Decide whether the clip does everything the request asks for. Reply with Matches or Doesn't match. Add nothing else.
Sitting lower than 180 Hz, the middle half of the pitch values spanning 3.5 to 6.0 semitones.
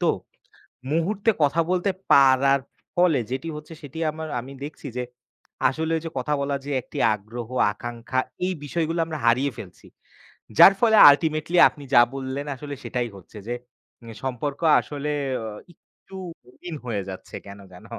Matches